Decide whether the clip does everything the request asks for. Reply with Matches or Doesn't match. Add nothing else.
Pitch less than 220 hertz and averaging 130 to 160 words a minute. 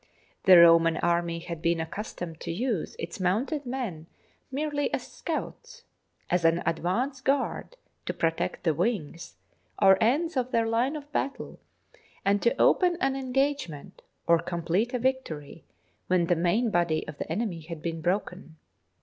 Matches